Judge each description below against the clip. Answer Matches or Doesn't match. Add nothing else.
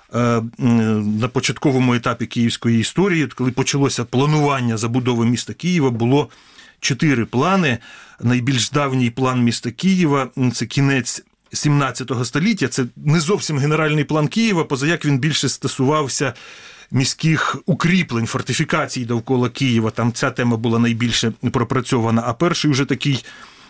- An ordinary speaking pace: Matches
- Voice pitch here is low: Matches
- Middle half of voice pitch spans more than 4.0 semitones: Doesn't match